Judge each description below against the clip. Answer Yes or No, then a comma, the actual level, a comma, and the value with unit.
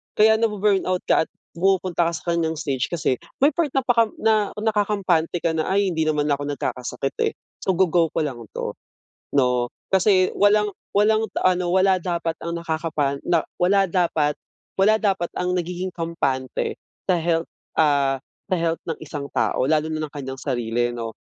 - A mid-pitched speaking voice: Yes, medium, 170 Hz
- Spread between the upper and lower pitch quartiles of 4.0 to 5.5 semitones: Yes, average, 4.6 semitones